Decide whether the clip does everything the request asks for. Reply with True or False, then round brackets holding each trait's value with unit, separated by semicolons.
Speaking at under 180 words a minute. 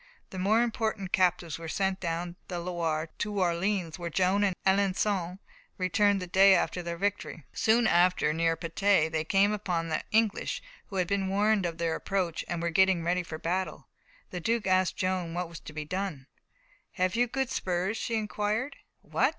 False (185 wpm)